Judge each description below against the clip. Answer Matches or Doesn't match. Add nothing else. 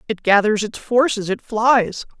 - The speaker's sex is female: Matches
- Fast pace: Doesn't match